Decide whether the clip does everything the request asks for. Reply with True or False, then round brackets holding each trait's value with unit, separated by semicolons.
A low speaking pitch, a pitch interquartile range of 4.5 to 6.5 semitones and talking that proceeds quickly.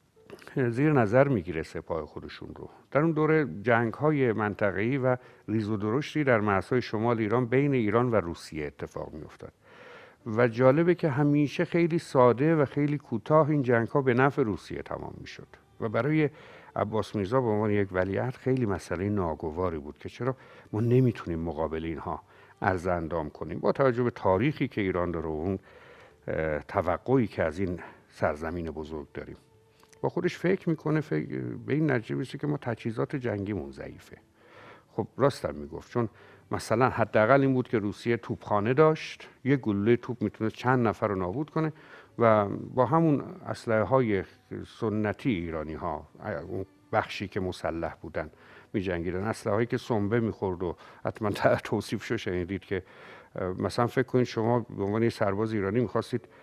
True (115 Hz; 5.2 semitones; 165 wpm)